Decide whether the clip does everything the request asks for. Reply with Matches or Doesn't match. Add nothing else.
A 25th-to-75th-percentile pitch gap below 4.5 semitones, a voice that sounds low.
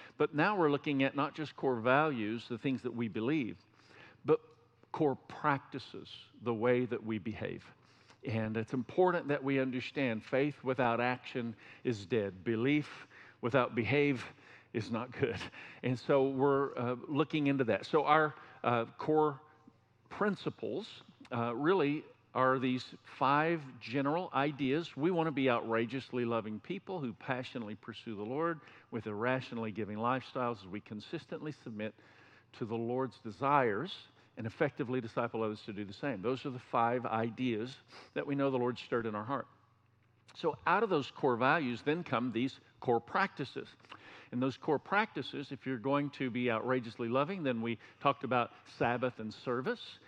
Matches